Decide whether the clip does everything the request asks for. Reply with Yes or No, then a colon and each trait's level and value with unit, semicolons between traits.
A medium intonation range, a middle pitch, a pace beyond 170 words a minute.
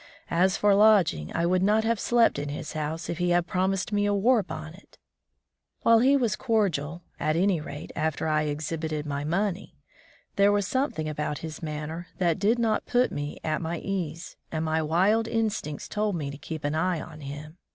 Yes: average, 5.0 semitones; medium, 170 Hz; average, 200 wpm